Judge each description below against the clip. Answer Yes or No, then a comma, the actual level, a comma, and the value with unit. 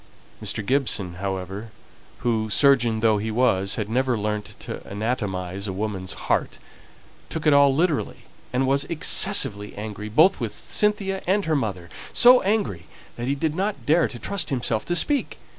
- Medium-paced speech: Yes, average, 160 wpm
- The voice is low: Yes, low, 120 Hz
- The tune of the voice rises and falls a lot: Yes, wide, 6.9 semitones